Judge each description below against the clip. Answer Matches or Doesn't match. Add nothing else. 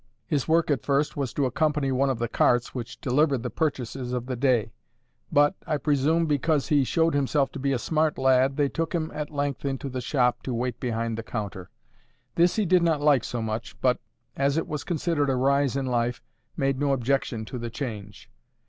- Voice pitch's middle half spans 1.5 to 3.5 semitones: Matches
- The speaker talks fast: Matches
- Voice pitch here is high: Doesn't match